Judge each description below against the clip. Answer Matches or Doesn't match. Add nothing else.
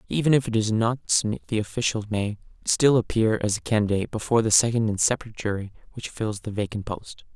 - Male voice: Matches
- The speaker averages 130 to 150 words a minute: Doesn't match